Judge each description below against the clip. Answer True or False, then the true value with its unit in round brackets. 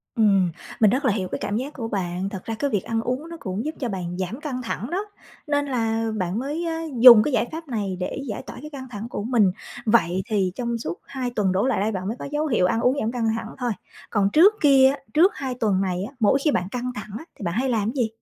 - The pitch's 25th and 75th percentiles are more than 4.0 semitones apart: True (5.0 semitones)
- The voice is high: True (230 Hz)